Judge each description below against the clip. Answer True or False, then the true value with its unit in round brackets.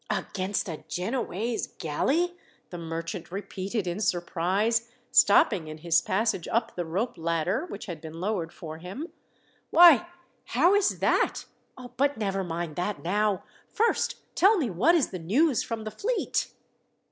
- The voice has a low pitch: False (200 Hz)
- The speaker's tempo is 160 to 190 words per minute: False (145 wpm)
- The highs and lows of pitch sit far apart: True (6.0 semitones)